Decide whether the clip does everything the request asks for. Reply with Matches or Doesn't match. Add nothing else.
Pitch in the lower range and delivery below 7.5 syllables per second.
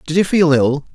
Doesn't match